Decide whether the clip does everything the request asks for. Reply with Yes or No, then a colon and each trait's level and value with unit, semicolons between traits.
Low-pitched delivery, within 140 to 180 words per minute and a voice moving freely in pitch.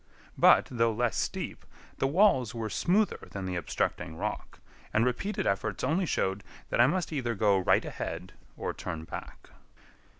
Yes: low, 115 Hz; average, 160 wpm; wide, 7.1 semitones